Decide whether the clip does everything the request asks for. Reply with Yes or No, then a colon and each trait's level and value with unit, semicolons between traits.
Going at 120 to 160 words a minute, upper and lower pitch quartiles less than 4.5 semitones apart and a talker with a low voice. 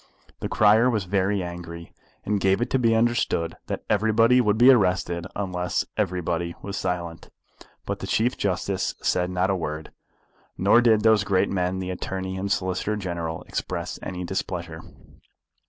Yes: average, 155 wpm; average, 3.1 semitones; very low, 95 Hz